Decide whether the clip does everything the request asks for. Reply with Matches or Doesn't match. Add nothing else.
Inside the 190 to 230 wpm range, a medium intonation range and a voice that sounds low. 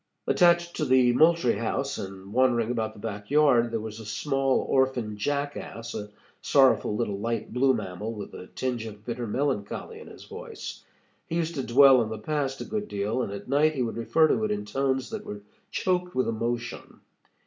Matches